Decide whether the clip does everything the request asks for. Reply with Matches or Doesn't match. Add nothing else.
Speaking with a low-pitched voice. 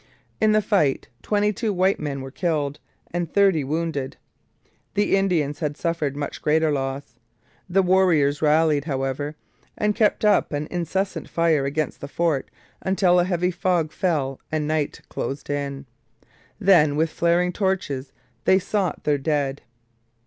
Doesn't match